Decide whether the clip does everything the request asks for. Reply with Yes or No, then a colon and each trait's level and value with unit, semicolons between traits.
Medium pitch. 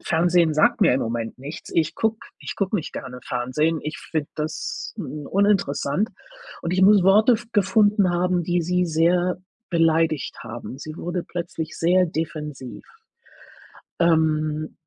Yes: medium, 165 Hz